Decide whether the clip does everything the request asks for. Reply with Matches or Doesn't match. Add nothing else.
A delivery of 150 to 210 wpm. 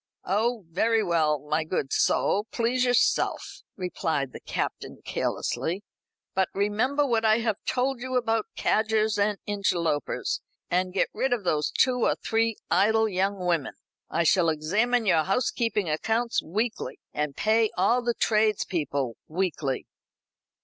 Doesn't match